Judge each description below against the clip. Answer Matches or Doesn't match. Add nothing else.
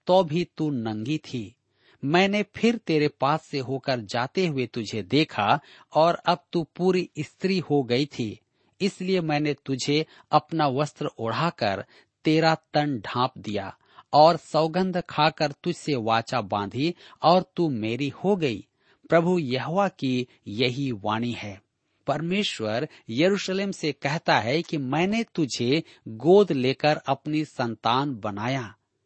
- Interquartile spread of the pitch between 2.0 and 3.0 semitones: Doesn't match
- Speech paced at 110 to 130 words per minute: Matches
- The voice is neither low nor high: Matches